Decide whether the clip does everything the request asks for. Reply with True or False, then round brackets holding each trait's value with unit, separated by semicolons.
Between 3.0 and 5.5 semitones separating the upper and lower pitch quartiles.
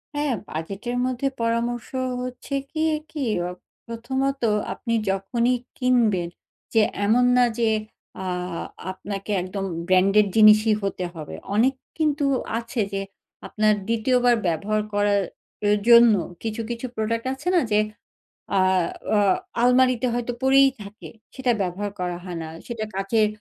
True (3.6 semitones)